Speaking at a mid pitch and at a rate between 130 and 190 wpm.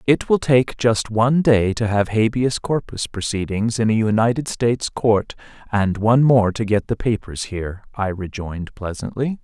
No: low, 110 Hz; average, 170 wpm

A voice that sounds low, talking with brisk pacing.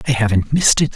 Yes: low, 120 Hz; fast, 250 wpm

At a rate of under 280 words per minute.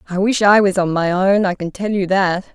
No: fast, 285 wpm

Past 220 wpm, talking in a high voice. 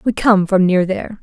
Yes: fast, 245 wpm; high, 195 Hz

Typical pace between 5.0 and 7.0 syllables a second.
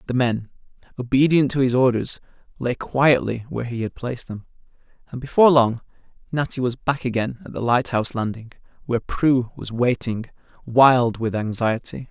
Yes: 5.3 syllables/s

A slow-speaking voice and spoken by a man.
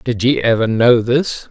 No: average, 200 wpm; male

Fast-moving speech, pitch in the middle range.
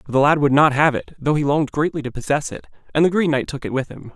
Yes: fast, 315 wpm; medium, 145 Hz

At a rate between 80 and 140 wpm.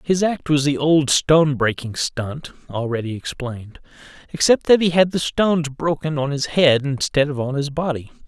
No: average, 180 wpm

